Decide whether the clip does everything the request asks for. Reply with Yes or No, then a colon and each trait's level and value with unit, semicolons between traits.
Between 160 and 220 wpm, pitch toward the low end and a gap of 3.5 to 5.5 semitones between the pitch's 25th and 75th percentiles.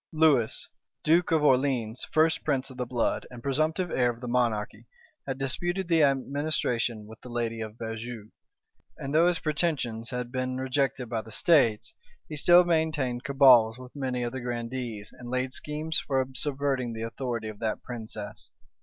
Yes: average, 170 wpm; low, 130 Hz; average, 3.9 semitones